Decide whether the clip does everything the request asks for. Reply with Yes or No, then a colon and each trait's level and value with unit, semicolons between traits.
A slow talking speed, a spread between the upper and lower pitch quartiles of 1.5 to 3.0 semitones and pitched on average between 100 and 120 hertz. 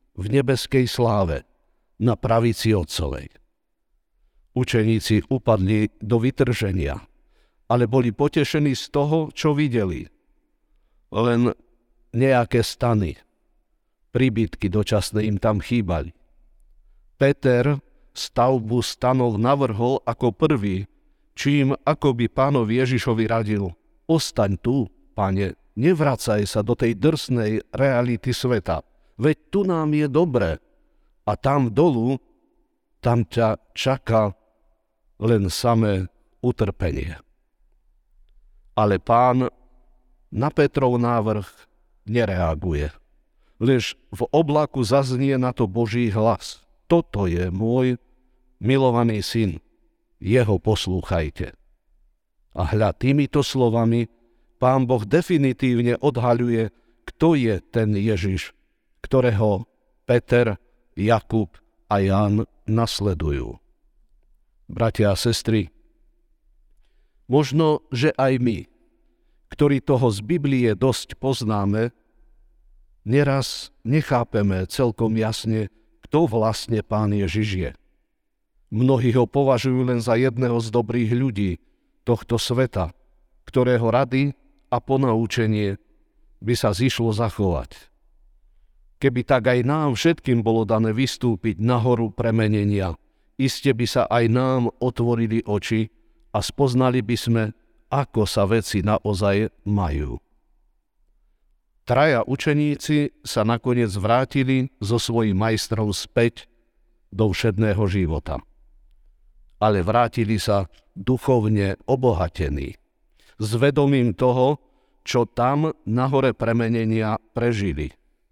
No: slow, 95 wpm; average, 3.6 semitones; low, 115 Hz